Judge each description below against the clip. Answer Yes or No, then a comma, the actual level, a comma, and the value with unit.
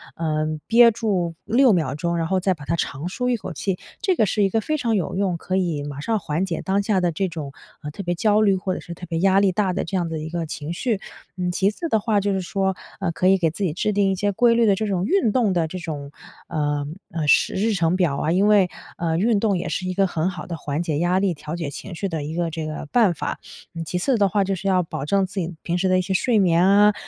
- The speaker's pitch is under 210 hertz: Yes, medium, 185 Hz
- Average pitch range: Yes, average, 3.5 semitones